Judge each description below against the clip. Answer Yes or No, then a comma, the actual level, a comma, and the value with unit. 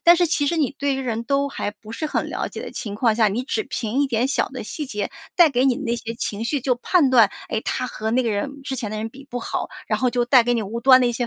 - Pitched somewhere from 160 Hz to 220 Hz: No, high, 245 Hz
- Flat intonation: No, average, 3.5 semitones